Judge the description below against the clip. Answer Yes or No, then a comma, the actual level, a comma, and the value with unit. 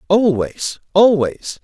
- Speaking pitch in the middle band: Yes, medium, 175 Hz